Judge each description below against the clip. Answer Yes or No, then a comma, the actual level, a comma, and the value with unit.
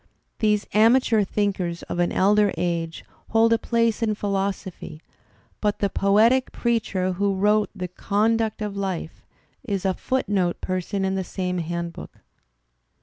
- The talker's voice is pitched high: Yes, high, 200 Hz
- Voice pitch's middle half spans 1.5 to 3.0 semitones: Yes, average, 2.7 semitones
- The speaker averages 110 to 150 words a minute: Yes, average, 140 wpm